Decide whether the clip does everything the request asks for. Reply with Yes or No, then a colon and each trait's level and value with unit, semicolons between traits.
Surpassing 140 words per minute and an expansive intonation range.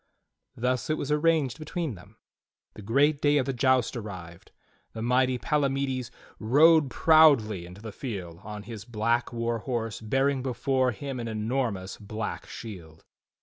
No: average, 150 wpm; average, 4.3 semitones